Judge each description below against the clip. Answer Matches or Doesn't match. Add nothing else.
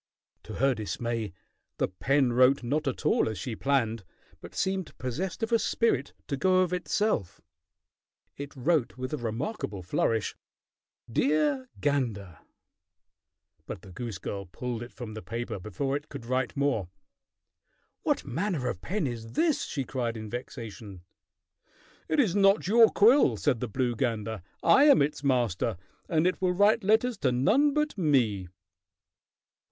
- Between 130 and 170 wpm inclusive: Matches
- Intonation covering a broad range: Matches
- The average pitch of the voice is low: Matches